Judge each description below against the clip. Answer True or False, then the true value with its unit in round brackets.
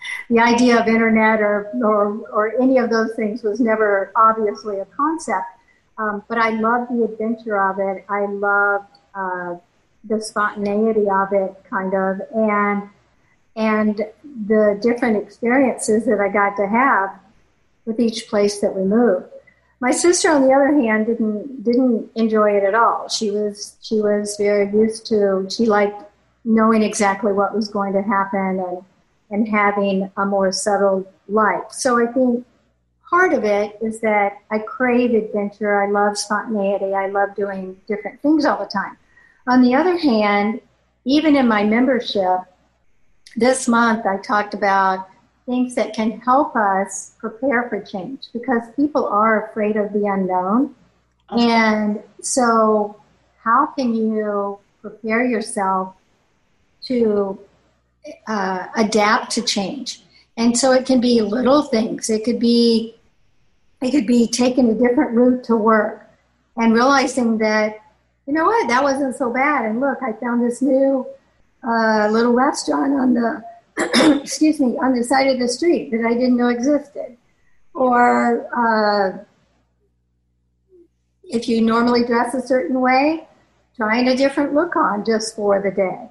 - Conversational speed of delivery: True (150 wpm)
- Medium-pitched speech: False (220 Hz)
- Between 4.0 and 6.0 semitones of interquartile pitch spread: False (3.3 semitones)